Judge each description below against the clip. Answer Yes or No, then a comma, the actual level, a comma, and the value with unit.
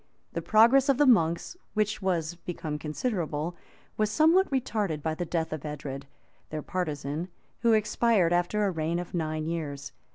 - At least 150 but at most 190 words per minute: Yes, average, 160 wpm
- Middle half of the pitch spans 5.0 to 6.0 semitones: Yes, wide, 5.5 semitones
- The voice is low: No, medium, 175 Hz